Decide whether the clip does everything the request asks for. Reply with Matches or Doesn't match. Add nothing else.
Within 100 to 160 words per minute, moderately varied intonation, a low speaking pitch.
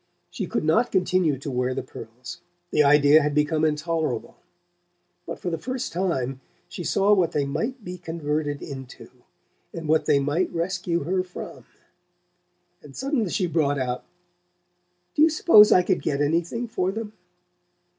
Doesn't match